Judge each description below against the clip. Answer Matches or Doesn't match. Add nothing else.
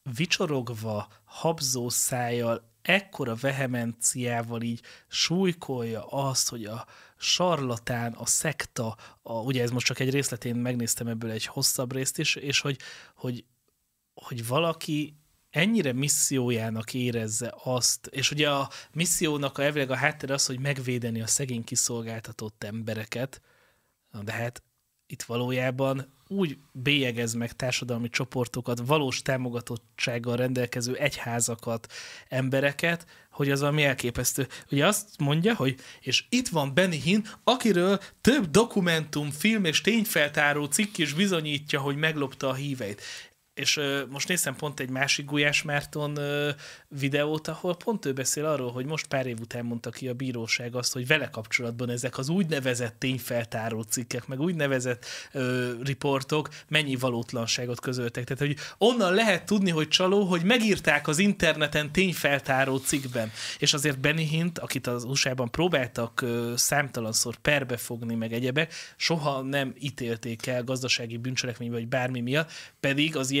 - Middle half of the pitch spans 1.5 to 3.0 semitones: Doesn't match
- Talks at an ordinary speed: Matches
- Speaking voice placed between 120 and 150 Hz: Matches